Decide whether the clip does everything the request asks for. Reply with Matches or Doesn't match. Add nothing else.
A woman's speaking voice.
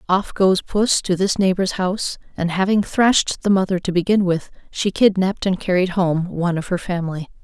Matches